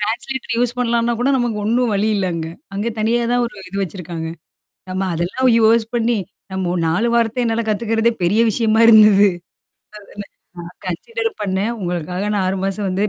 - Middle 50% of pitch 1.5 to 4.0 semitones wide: Yes, average, 3.6 semitones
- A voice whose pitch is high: Yes, high, 215 Hz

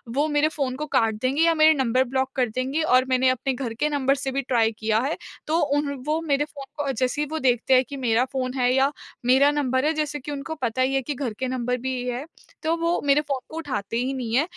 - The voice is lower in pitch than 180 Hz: No, very high, 265 Hz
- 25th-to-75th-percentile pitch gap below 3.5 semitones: Yes, narrow, 2.6 semitones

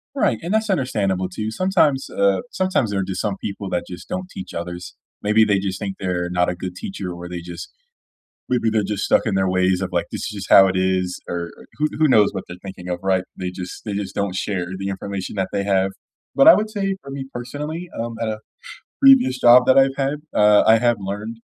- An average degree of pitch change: No, wide, 5.7 semitones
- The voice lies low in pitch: Yes, low, 100 Hz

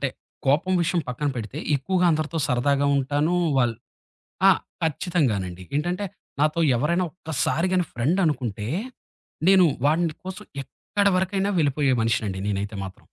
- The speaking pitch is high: No, medium, 150 Hz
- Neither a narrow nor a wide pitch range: No, wide, 6.4 semitones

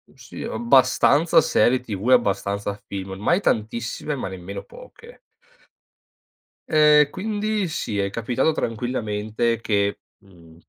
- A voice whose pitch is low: Yes, low, 115 Hz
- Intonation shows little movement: No, wide, 6.7 semitones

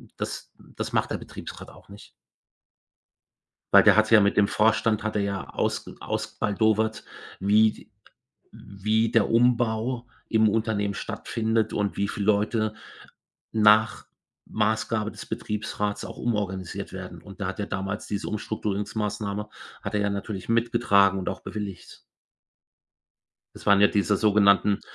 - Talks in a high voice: No, low, 105 Hz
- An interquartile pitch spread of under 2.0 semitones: Yes, narrow, 1.6 semitones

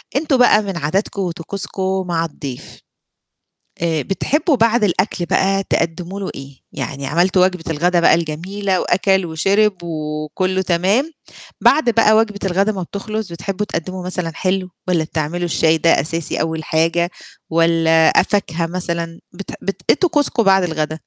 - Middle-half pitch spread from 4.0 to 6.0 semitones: No, average, 3.2 semitones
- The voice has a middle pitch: Yes, medium, 180 Hz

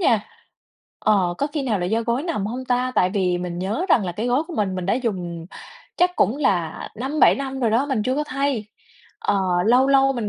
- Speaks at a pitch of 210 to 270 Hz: Yes, high, 235 Hz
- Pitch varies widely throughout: Yes, wide, 5.8 semitones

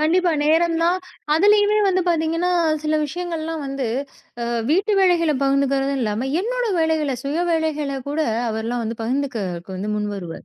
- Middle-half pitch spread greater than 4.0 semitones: Yes, average, 4.8 semitones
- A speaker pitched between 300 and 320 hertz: Yes, very high, 305 Hz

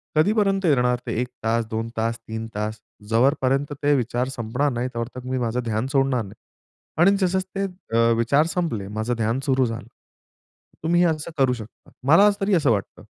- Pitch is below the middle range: Yes, low, 125 Hz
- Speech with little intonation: No, average, 4.5 semitones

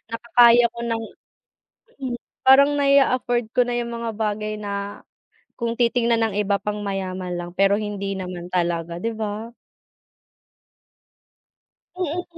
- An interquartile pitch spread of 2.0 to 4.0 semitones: Yes, average, 3.2 semitones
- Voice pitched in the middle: No, high, 215 Hz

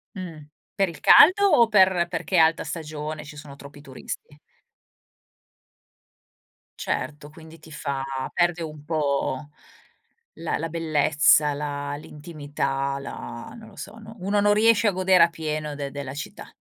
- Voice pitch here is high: No, medium, 155 Hz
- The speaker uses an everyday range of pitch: Yes, average, 3.5 semitones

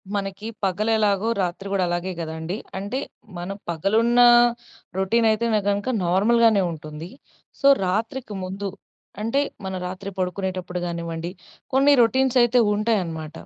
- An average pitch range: Yes, average, 4.0 semitones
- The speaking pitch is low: No, high, 195 Hz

